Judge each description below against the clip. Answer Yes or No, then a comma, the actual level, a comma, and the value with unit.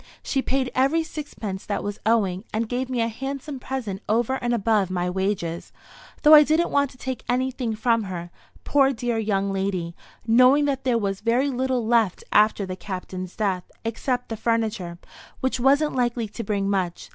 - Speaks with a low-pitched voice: No, high, 230 Hz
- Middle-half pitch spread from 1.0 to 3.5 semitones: No, average, 4.8 semitones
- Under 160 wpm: No, average, 180 wpm